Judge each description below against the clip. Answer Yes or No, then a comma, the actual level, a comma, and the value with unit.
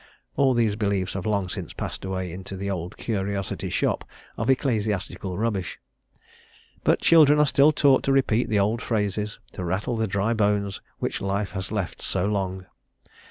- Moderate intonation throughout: Yes, average, 3.1 semitones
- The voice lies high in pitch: No, low, 100 Hz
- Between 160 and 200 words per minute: Yes, average, 165 wpm